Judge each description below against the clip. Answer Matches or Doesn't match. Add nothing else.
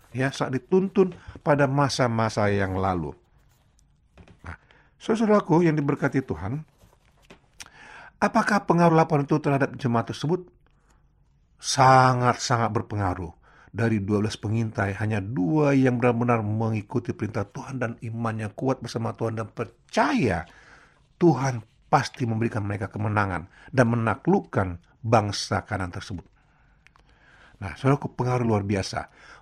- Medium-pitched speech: Doesn't match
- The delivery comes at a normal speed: Matches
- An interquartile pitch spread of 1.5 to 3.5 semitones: Doesn't match